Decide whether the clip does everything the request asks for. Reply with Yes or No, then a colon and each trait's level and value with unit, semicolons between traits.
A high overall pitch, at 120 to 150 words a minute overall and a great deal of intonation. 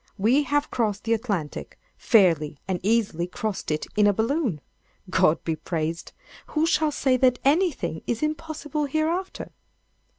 Yes: high, 230 Hz; slow, 135 wpm; wide, 8.6 semitones